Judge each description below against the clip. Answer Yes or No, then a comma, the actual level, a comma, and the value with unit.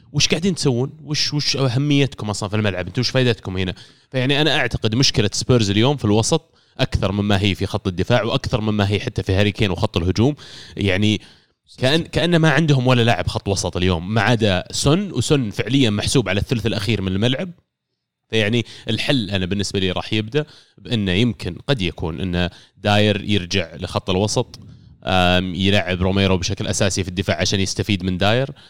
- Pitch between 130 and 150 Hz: No, low, 110 Hz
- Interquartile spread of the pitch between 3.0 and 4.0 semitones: No, average, 4.9 semitones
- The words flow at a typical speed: No, fast, 170 wpm